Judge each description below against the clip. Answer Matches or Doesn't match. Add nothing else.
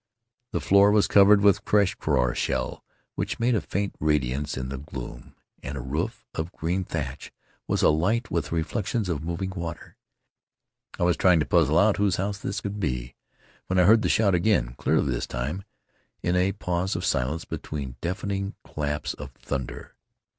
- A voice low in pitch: Matches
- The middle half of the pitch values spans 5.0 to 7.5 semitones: Matches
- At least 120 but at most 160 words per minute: Doesn't match